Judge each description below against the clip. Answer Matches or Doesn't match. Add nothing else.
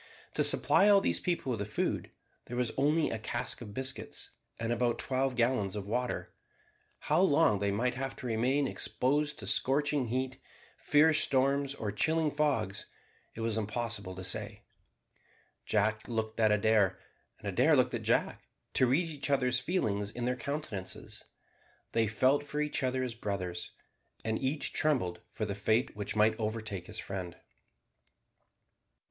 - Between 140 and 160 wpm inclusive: Matches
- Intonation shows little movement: Doesn't match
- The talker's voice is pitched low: Matches